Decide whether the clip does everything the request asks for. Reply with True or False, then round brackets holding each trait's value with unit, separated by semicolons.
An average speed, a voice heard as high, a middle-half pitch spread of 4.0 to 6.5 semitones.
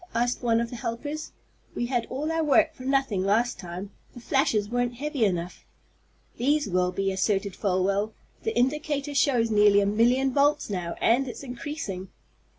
True (165 wpm; 240 Hz; 5.4 semitones)